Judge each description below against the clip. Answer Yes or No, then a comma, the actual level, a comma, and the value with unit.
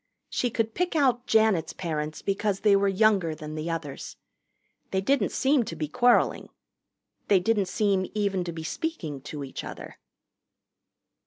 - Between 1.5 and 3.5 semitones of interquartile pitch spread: No, wide, 5.6 semitones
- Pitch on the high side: Yes, high, 195 Hz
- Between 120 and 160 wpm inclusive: Yes, average, 155 wpm